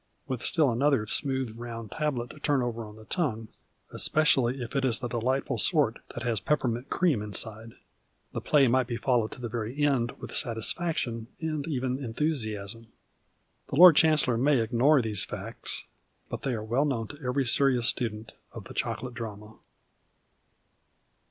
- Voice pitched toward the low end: Yes, low, 125 Hz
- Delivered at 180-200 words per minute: No, average, 165 wpm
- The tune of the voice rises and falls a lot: No, average, 3.6 semitones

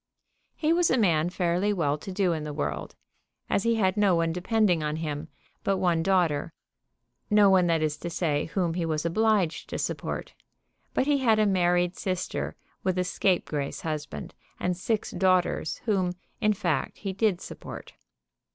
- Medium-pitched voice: Yes, medium, 180 Hz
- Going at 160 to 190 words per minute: Yes, average, 170 wpm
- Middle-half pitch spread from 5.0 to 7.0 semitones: No, average, 3.5 semitones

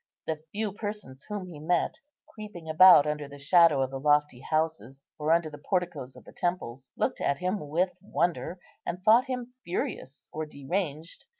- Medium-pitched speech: Yes, medium, 160 Hz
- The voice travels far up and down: No, average, 4.1 semitones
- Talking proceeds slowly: No, average, 175 wpm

